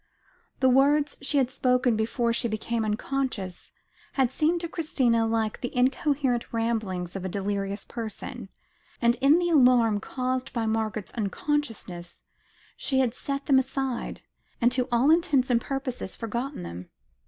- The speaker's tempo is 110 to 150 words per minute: Yes, average, 145 wpm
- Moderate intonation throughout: Yes, average, 3.6 semitones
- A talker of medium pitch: No, high, 245 Hz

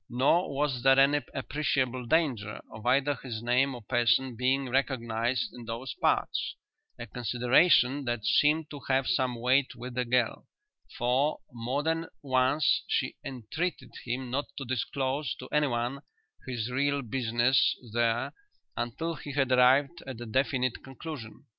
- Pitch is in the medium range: No, low, 130 Hz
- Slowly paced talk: No, average, 145 wpm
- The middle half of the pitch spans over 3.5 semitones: No, narrow, 2.5 semitones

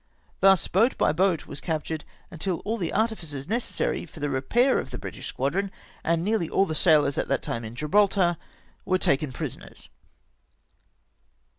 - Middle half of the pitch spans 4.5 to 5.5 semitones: Yes, average, 5.2 semitones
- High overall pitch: No, medium, 165 Hz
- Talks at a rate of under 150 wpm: No, average, 160 wpm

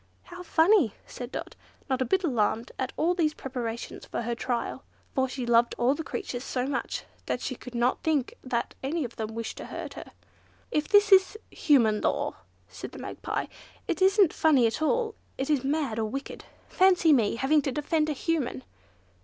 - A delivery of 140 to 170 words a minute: No, average, 190 wpm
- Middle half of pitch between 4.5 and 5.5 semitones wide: Yes, average, 5.2 semitones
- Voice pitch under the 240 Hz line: No, very high, 270 Hz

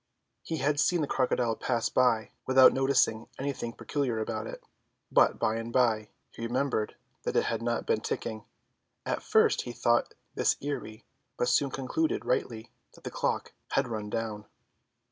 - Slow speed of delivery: No, average, 165 wpm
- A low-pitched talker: Yes, low, 120 Hz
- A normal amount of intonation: Yes, average, 3.3 semitones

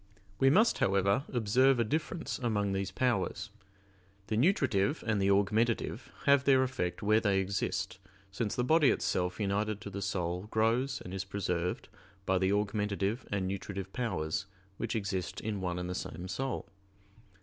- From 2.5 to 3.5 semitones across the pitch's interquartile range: No, average, 4.0 semitones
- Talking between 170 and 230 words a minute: No, average, 160 wpm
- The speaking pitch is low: Yes, low, 105 Hz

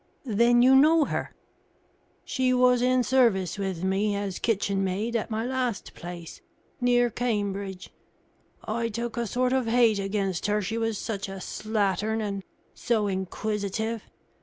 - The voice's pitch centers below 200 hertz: No, high, 220 Hz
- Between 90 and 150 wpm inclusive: Yes, average, 140 wpm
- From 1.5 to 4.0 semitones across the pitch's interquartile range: Yes, average, 3.5 semitones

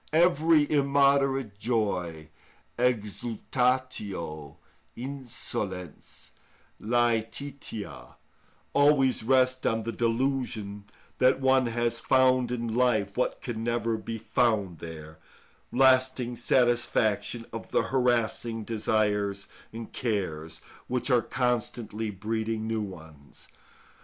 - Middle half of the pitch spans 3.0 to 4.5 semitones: Yes, average, 3.6 semitones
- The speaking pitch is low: Yes, low, 115 Hz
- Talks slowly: Yes, slow, 90 wpm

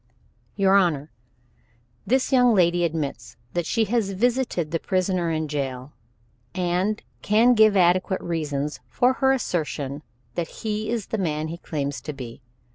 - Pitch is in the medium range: Yes, medium, 180 Hz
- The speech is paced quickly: No, average, 150 wpm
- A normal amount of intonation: No, wide, 5.9 semitones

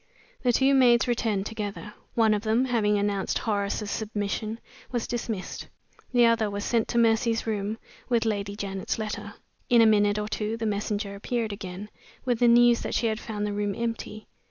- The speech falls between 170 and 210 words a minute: Yes, average, 180 wpm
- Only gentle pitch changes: Yes, narrow, 2.1 semitones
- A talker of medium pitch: No, high, 220 Hz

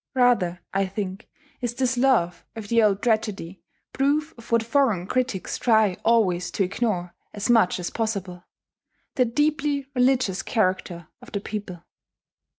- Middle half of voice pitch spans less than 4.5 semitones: No, average, 4.8 semitones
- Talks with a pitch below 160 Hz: No, high, 220 Hz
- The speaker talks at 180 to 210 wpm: No, average, 145 wpm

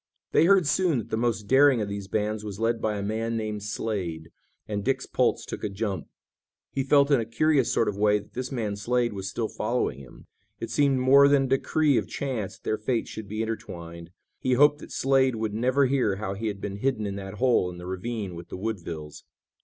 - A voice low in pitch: Yes, low, 110 Hz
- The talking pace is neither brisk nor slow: No, fast, 225 wpm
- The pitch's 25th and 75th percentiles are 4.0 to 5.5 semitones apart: Yes, average, 4.4 semitones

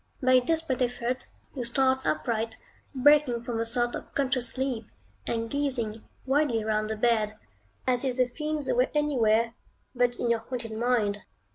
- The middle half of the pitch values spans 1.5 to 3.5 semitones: Yes, average, 2.7 semitones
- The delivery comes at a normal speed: Yes, average, 160 wpm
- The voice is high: Yes, high, 245 Hz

